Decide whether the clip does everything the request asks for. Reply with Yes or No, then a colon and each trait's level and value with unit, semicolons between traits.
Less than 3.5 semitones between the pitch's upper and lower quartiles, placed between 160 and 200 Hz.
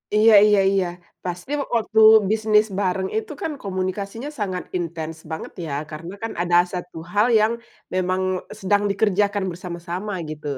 Yes: average, 3.0 semitones; high, 190 Hz